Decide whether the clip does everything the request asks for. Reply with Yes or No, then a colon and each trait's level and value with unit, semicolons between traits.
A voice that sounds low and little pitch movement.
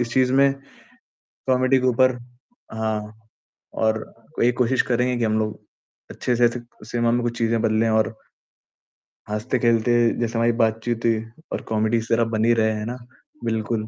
Yes: low, 115 Hz; narrow, 1.7 semitones